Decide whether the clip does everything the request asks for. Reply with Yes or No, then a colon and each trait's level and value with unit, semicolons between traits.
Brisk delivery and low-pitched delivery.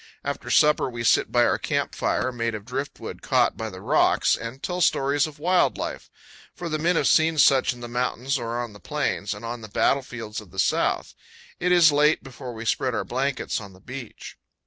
Yes: fast, 215 wpm; low, 130 Hz